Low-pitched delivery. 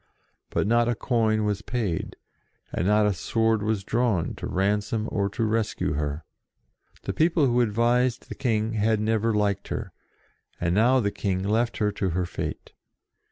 Yes: low, 110 Hz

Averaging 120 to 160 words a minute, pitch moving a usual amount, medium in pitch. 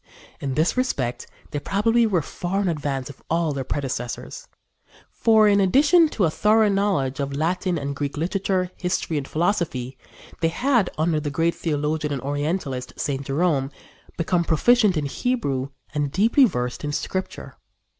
No: average, 155 wpm; wide, 5.9 semitones; medium, 165 Hz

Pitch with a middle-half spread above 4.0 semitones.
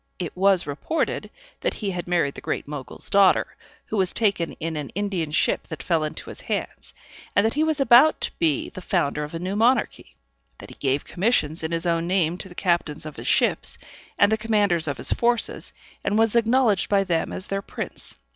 Yes: average, 4.6 semitones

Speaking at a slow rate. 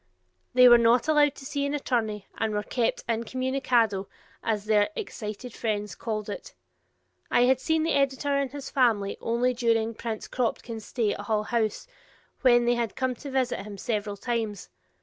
No: average, 175 wpm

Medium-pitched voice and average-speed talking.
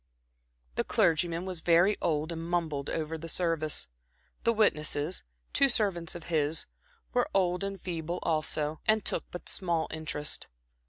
Yes: medium, 170 Hz; average, 145 wpm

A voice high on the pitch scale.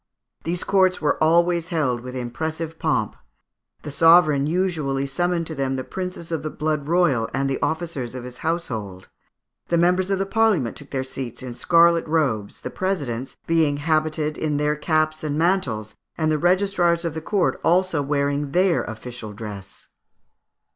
No: medium, 155 Hz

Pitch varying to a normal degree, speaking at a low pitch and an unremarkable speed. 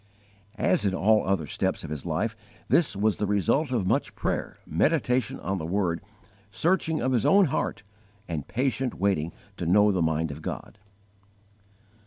No: wide, 6.8 semitones; low, 100 Hz; average, 165 wpm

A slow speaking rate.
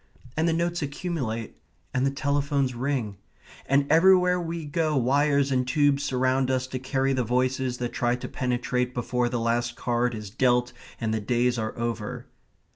No: average, 170 wpm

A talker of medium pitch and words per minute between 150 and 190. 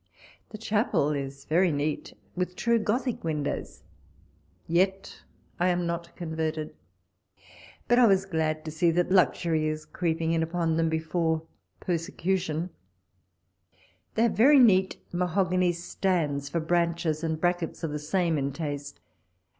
No: medium, 170 Hz; average, 140 wpm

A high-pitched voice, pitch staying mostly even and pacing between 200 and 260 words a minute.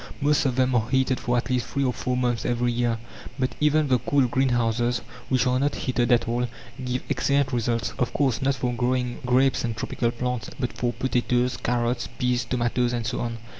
No: low, 125 Hz; narrow, 1.3 semitones; fast, 205 wpm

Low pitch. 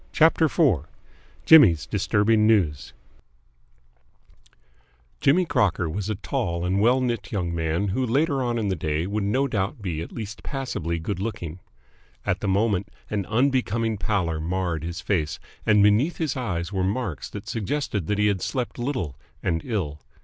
Yes: low, 105 Hz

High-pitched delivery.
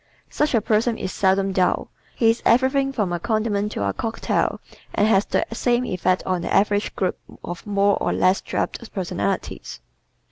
Yes: high, 205 Hz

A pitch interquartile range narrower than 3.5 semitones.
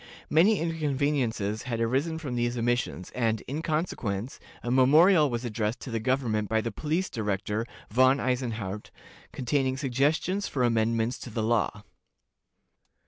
No: average, 4.2 semitones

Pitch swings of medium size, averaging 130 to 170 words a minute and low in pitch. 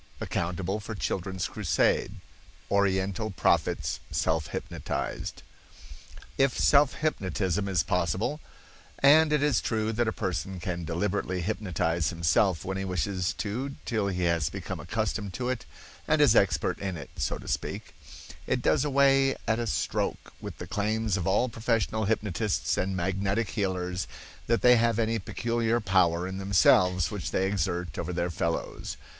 Yes: average, 3.8 semitones; average, 150 wpm; low, 100 Hz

